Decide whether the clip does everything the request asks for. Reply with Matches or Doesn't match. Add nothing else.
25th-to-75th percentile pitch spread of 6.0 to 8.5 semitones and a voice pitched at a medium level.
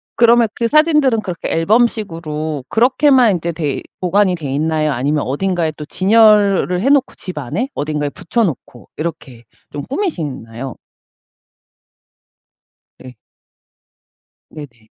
Matches